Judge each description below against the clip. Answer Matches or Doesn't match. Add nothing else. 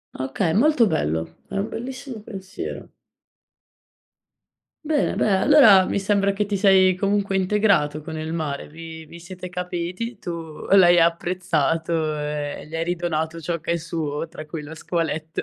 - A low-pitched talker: Doesn't match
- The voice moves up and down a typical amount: Matches